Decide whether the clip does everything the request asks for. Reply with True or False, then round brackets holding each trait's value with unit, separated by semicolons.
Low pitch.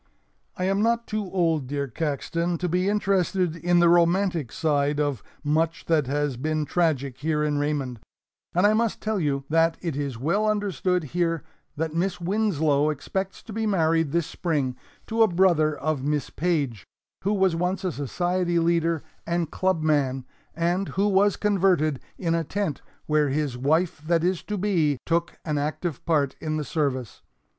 False (165 Hz)